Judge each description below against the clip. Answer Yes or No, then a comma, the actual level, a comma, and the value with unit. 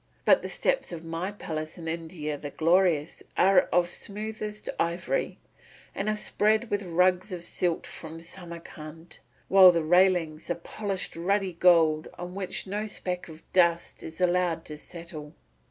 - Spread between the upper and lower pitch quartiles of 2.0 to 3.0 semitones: Yes, narrow, 2.6 semitones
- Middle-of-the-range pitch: Yes, medium, 175 Hz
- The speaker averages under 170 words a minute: Yes, average, 155 wpm